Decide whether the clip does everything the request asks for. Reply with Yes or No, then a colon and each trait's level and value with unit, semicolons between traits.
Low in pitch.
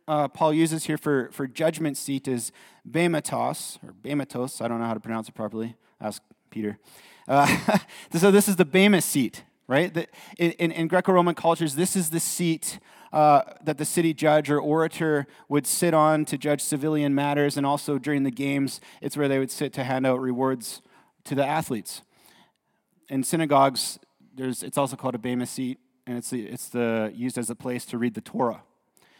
No: medium, 145 Hz